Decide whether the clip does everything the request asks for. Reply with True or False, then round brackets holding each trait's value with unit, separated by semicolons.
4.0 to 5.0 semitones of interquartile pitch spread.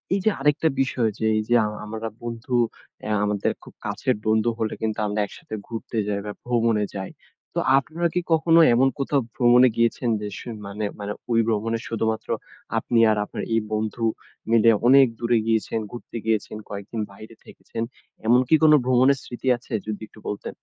False (2.6 semitones)